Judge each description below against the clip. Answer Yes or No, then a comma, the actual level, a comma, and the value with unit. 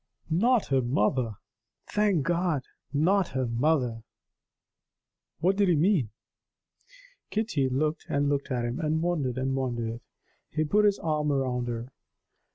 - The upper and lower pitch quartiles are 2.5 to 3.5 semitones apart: No, average, 5.3 semitones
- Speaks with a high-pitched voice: No, medium, 145 Hz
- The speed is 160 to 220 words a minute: No, slow, 135 wpm